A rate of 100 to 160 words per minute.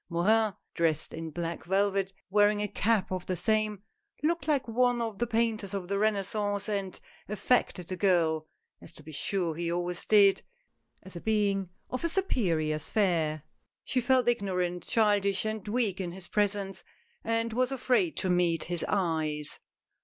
No: average, 170 wpm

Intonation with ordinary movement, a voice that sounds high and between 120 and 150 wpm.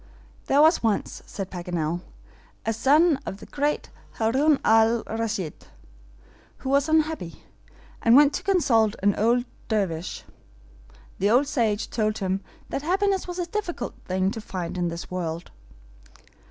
No: wide, 7.3 semitones; high, 225 Hz; average, 140 wpm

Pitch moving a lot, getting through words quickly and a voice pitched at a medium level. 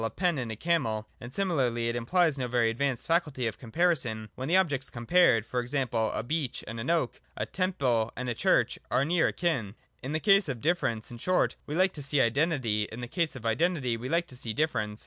No: wide, 6.2 semitones; fast, 225 wpm; low, 130 Hz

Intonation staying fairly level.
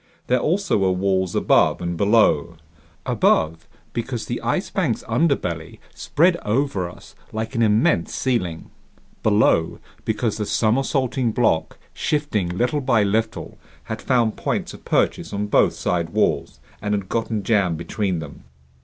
No: average, 4.8 semitones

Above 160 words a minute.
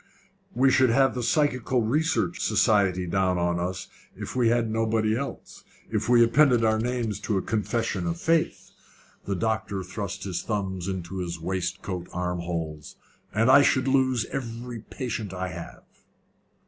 No: average, 155 wpm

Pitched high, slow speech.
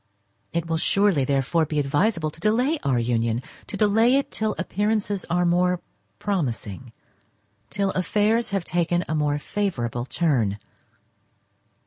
No: medium, 170 Hz; slow, 120 wpm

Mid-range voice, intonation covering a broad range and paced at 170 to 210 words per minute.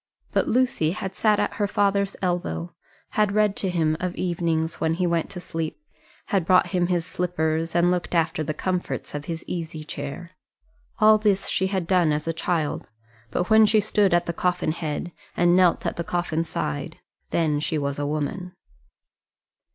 No: medium, 175 Hz; average, 2.9 semitones; average, 180 wpm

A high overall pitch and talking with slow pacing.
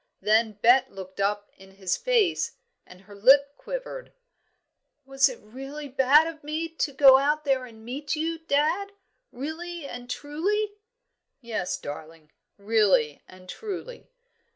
Yes: very high, 270 Hz; slow, 130 wpm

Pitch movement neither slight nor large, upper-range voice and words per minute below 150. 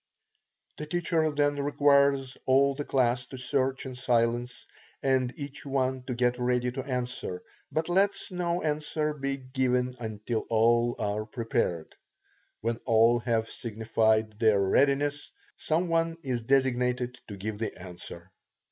No: average, 3.4 semitones; low, 125 Hz; average, 140 wpm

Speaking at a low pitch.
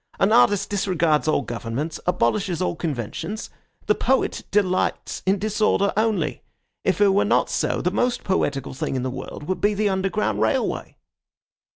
No: high, 190 Hz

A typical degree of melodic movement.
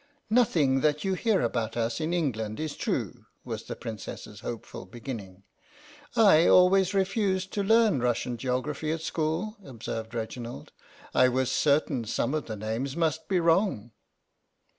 No: wide, 7.9 semitones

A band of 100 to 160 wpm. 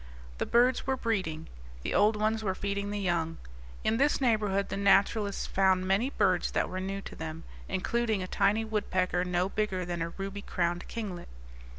No: average, 180 wpm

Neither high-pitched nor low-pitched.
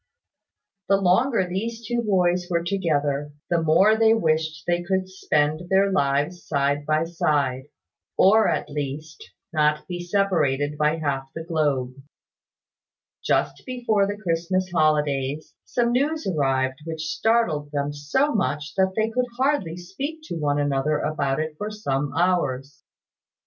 Yes: medium, 165 Hz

